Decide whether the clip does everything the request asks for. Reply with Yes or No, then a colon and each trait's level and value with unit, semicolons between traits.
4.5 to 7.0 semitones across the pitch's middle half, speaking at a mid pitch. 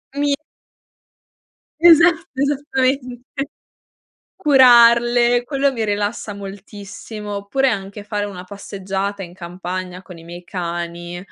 No: wide, 5.4 semitones; high, 205 Hz